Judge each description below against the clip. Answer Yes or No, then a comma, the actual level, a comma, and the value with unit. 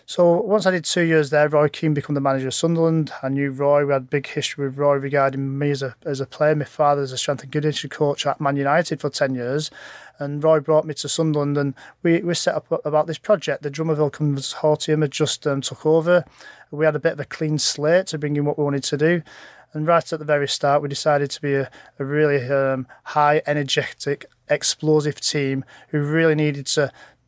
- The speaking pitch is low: No, medium, 150 Hz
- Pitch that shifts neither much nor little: No, narrow, 1.7 semitones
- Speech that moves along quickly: Yes, fast, 230 wpm